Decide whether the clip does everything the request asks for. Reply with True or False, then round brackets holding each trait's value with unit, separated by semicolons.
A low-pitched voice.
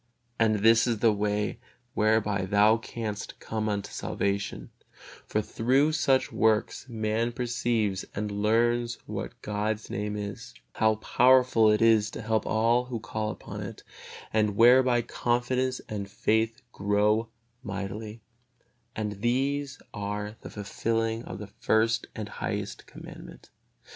True (110 Hz)